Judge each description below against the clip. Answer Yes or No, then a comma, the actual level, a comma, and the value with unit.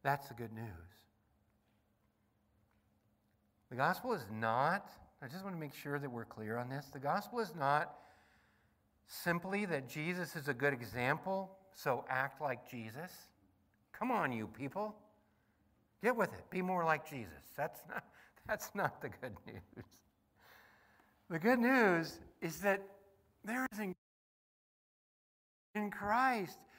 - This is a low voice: No, medium, 145 Hz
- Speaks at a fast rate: No, slow, 135 wpm